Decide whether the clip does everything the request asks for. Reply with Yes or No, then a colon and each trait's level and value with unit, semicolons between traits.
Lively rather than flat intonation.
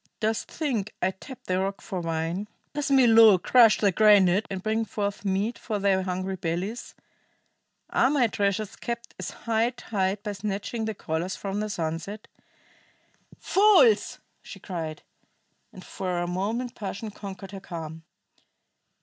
No: average, 3.2 semitones